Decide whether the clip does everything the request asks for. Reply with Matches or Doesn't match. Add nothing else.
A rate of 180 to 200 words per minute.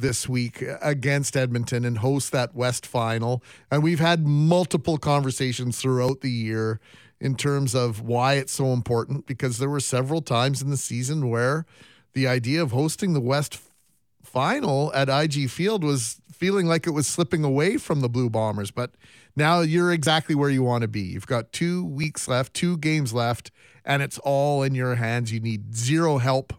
Matches